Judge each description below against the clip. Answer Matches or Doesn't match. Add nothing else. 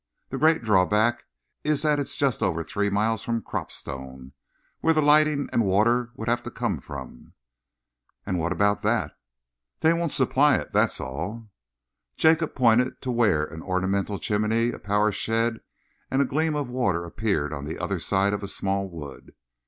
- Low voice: Matches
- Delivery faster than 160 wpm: Matches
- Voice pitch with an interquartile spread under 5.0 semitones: Doesn't match